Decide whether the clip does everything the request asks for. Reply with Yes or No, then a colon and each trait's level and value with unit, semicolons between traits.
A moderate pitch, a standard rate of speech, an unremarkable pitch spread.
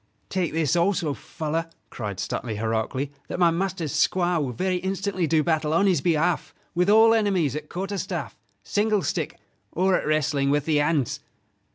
Yes: medium, 165 Hz; average, 170 wpm; average, 4.2 semitones